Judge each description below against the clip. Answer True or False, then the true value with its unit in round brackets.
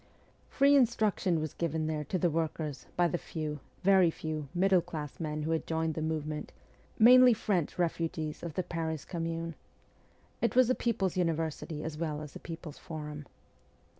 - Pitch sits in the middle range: True (165 Hz)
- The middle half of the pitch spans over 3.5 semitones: False (2.8 semitones)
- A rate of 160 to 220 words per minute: True (165 wpm)